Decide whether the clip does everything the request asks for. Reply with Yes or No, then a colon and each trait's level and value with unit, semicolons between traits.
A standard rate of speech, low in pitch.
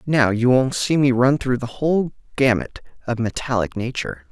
Yes: average, 180 wpm; low, 125 Hz